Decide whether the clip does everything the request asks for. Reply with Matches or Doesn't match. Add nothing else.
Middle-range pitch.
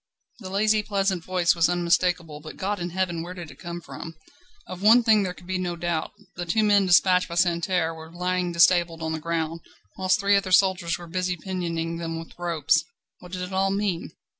Matches